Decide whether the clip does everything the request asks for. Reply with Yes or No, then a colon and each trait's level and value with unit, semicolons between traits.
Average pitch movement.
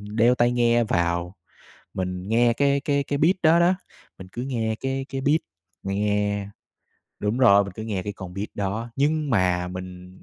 No: wide, 5.9 semitones